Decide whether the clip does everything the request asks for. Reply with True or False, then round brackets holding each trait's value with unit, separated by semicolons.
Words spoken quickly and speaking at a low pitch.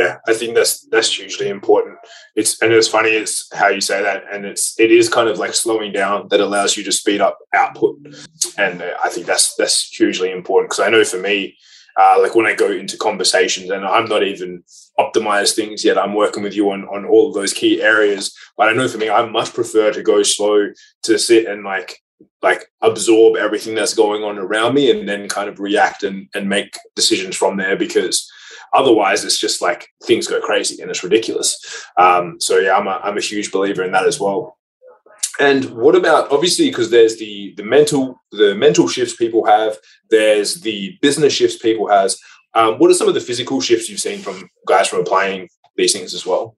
False (215 wpm; 385 Hz)